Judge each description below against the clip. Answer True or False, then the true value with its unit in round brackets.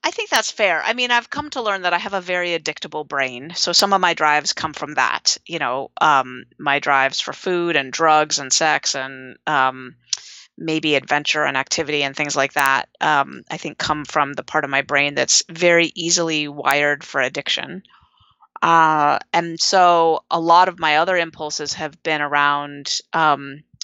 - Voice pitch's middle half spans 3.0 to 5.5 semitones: True (3.3 semitones)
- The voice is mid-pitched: True (155 Hz)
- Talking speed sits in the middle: True (190 wpm)